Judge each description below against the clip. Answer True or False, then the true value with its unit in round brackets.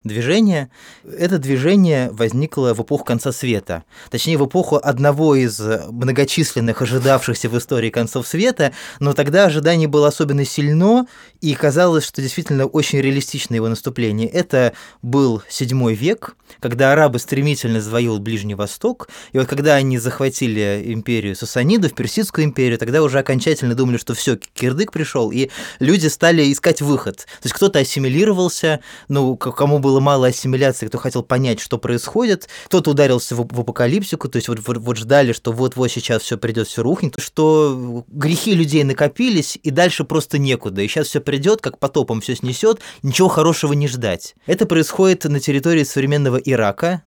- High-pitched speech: False (135 Hz)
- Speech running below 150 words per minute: False (160 wpm)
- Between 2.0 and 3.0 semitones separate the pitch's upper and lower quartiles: False (4.4 semitones)